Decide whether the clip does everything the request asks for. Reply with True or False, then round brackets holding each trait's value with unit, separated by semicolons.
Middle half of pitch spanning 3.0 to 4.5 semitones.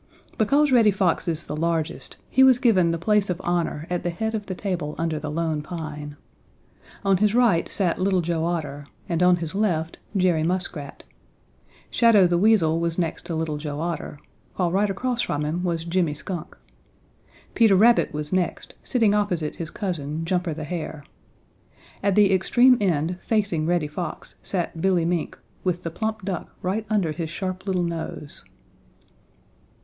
True (3.5 semitones)